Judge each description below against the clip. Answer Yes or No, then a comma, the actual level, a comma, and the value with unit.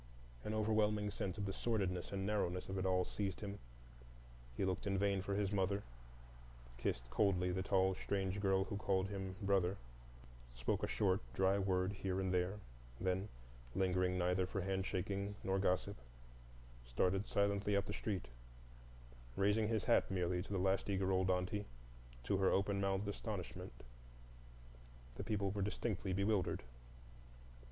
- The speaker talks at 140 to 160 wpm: Yes, average, 150 wpm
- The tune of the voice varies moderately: No, narrow, 1.4 semitones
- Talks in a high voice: No, very low, 95 Hz